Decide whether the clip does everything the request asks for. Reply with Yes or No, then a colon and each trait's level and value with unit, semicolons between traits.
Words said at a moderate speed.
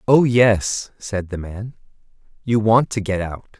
Yes: average, 165 wpm